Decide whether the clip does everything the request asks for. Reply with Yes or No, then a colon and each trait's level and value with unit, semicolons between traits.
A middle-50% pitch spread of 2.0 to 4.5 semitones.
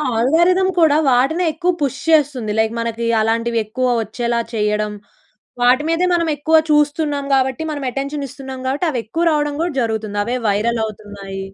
No: average, 4.9 semitones